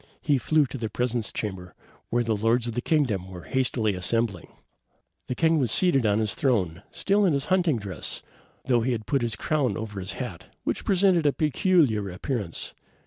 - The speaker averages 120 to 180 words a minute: No, average, 195 wpm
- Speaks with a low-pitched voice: Yes, low, 120 Hz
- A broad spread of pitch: Yes, wide, 5.8 semitones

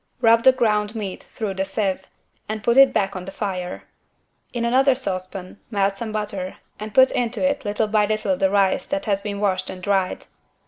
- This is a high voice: Yes, high, 210 Hz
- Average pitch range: Yes, average, 3.1 semitones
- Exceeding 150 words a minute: Yes, average, 195 wpm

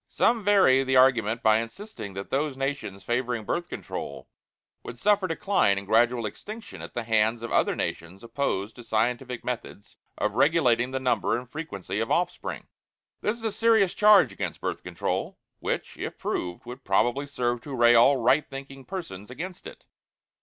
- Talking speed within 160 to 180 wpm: Yes, average, 170 wpm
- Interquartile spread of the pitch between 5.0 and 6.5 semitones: Yes, wide, 5.4 semitones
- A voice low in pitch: Yes, low, 125 Hz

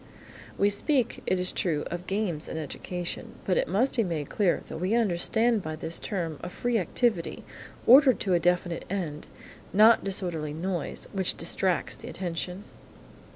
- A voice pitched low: No, medium, 185 Hz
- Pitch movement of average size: Yes, average, 3.8 semitones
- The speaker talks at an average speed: Yes, average, 160 wpm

